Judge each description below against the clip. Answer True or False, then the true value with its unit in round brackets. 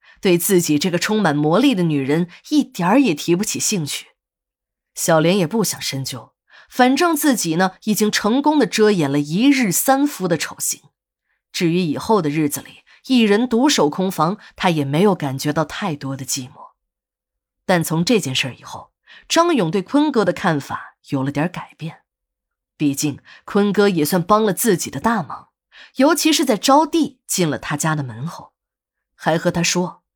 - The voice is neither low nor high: True (180 Hz)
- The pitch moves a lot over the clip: True (7.2 semitones)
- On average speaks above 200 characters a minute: True (250 characters per minute)